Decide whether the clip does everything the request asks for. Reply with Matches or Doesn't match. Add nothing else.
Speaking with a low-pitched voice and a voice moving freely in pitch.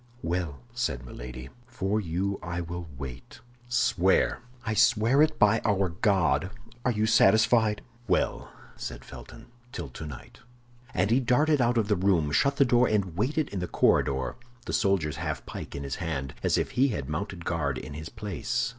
Matches